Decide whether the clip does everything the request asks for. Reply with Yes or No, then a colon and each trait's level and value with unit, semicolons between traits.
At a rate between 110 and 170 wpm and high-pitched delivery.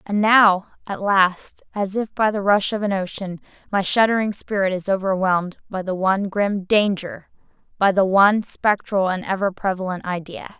Yes: average, 165 wpm; high, 195 Hz